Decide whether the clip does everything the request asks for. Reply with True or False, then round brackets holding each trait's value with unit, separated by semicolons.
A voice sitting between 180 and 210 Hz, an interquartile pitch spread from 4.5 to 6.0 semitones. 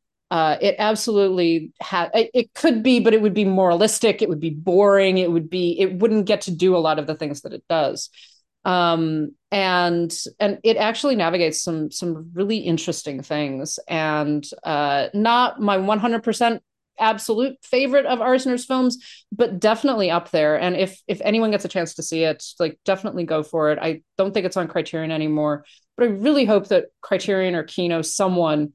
True (185 Hz; 5.2 semitones)